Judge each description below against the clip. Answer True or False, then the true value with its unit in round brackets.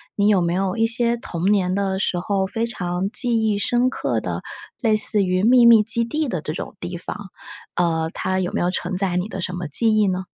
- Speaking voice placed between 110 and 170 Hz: False (195 Hz)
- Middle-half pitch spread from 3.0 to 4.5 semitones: True (3.9 semitones)